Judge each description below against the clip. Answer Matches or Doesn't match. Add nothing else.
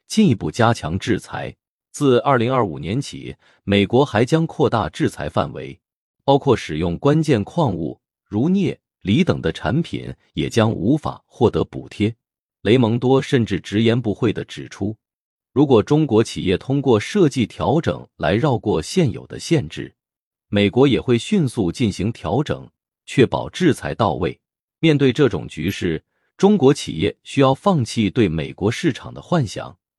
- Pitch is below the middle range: Matches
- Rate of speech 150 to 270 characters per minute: Matches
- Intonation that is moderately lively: Doesn't match